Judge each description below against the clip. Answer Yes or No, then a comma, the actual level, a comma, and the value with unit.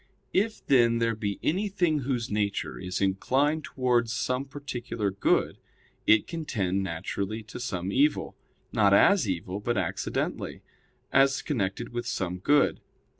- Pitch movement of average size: No, wide, 5.7 semitones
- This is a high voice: No, low, 120 Hz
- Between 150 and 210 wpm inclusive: No, slow, 135 wpm